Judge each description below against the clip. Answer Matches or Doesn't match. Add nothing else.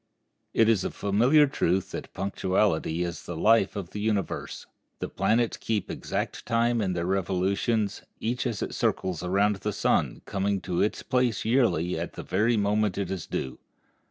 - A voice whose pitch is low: Matches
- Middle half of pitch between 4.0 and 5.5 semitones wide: Doesn't match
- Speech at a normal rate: Matches